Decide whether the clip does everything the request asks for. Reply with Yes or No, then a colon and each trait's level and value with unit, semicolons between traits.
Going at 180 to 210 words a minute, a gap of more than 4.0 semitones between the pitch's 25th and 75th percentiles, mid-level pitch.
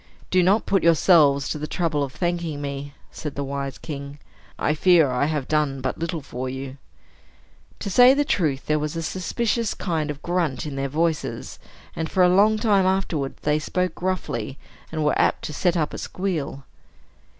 Yes: average, 190 wpm; average, 4.5 semitones; medium, 155 Hz